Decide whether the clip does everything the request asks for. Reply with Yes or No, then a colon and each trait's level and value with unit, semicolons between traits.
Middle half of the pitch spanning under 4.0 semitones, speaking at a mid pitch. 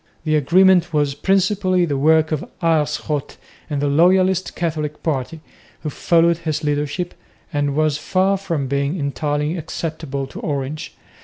Yes: average, 3.0 semitones; medium, 155 Hz